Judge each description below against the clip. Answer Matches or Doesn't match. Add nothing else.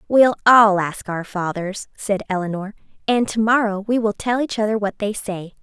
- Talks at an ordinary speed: Matches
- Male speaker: Doesn't match